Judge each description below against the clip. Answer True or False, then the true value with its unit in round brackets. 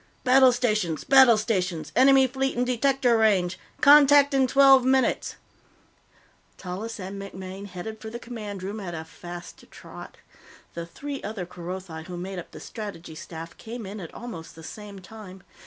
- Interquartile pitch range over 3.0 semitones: True (5.6 semitones)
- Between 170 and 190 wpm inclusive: False (160 wpm)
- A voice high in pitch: True (210 Hz)